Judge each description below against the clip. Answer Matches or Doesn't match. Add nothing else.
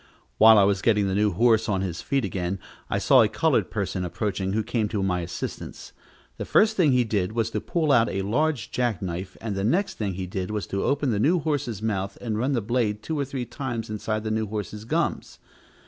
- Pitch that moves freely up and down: Doesn't match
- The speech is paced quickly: Matches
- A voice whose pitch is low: Matches